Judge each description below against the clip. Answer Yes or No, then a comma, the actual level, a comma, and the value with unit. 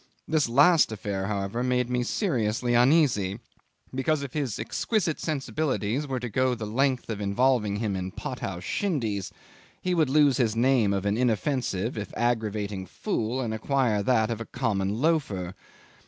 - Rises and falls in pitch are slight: No, average, 4.6 semitones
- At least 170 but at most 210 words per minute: No, average, 160 wpm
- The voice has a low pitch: Yes, low, 120 Hz